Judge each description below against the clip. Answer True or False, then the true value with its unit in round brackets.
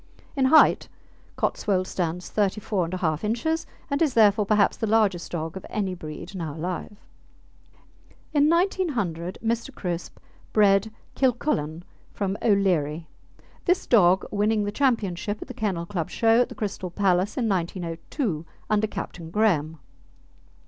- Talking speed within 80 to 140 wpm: True (135 wpm)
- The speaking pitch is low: False (200 Hz)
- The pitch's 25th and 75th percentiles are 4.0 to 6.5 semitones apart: True (4.4 semitones)